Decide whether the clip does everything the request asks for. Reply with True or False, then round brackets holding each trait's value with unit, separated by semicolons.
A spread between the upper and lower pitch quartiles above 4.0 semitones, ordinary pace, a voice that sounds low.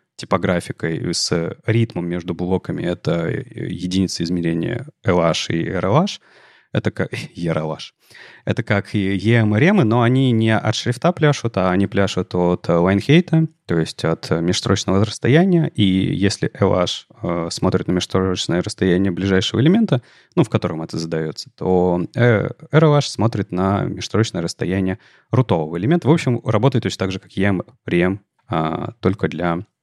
True (5.2 semitones; 140 wpm; 100 Hz)